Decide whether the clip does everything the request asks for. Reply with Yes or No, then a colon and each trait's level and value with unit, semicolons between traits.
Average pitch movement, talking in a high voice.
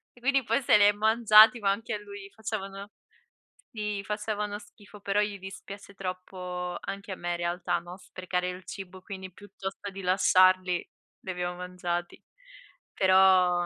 No: narrow, 2.2 semitones; high, 195 Hz